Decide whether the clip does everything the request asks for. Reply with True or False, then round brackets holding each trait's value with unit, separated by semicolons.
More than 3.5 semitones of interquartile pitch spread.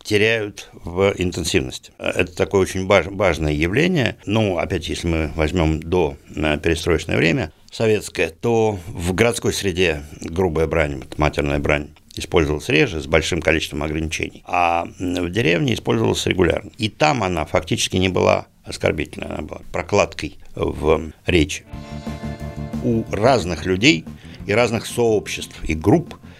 True (5.0 semitones)